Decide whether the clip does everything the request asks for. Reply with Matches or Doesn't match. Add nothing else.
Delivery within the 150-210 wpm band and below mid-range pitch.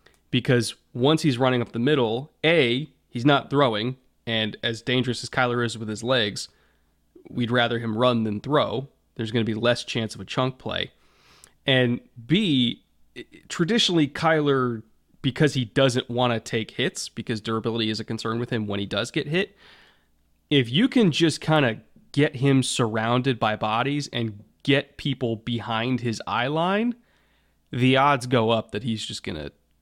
Matches